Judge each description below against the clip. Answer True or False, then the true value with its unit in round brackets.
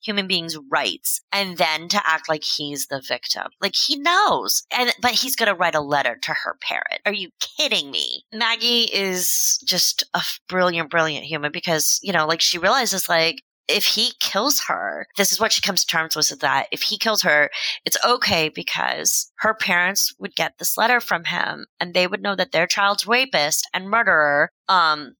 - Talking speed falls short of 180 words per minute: False (200 wpm)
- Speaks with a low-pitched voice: False (190 Hz)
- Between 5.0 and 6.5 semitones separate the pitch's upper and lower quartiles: True (5.5 semitones)